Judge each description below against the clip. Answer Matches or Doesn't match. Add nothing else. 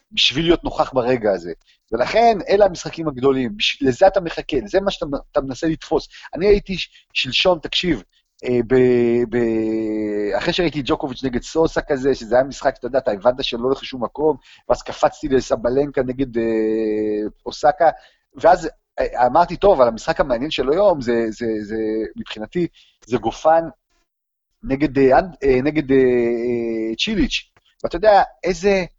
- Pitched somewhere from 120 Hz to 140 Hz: Matches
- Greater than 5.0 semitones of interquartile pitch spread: Matches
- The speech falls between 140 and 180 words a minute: Matches